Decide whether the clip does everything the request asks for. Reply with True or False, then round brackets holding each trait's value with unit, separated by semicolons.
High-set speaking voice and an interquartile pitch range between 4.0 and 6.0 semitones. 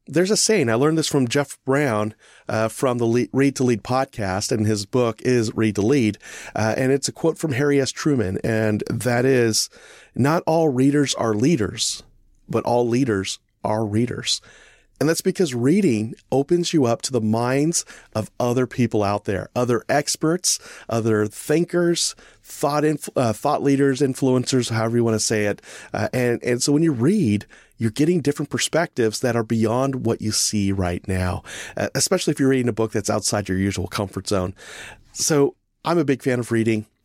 False (120 Hz; 4.7 semitones)